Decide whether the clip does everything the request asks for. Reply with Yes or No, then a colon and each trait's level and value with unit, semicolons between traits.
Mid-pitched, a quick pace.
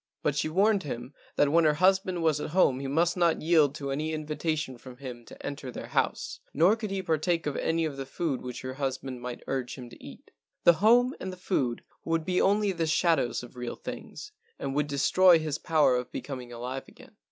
Yes: medium, 150 Hz; fast, 225 wpm